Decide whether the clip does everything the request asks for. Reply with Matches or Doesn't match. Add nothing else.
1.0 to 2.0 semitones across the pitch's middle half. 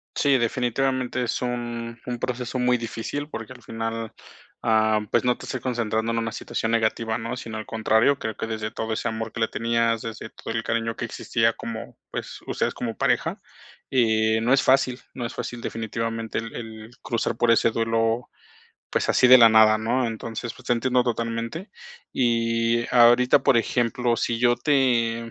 Matches